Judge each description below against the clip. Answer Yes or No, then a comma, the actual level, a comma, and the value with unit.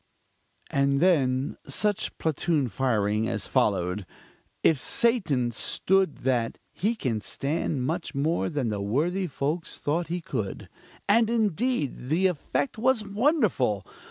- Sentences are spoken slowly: Yes, slow, 125 wpm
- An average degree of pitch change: No, wide, 7.2 semitones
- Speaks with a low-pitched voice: No, medium, 155 Hz